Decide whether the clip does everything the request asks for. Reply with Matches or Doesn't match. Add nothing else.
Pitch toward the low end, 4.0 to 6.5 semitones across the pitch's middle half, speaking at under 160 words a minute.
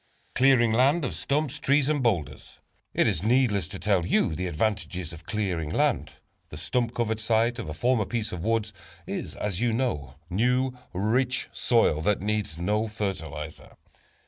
Doesn't match